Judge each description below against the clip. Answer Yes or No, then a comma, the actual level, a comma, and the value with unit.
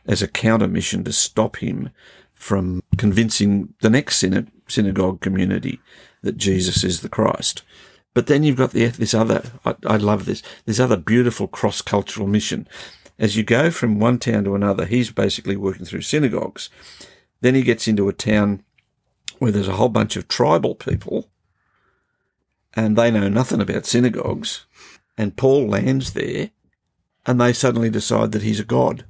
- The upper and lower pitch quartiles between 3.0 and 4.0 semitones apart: Yes, average, 3.3 semitones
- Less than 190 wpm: Yes, average, 165 wpm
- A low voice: Yes, low, 110 Hz